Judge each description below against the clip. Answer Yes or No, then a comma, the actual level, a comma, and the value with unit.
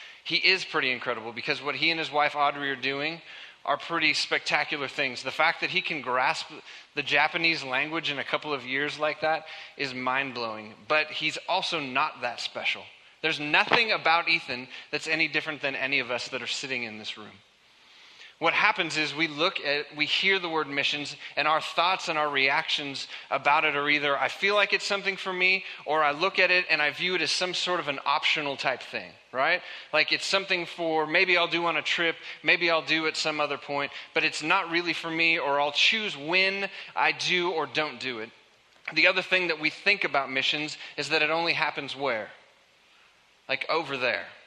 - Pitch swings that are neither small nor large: Yes, average, 3.0 semitones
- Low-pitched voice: No, medium, 155 Hz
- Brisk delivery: Yes, fast, 210 wpm